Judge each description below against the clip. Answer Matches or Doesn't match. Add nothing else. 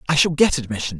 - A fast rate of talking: Matches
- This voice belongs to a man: Matches